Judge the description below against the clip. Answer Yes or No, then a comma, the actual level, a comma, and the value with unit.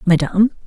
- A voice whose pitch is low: No, medium, 185 Hz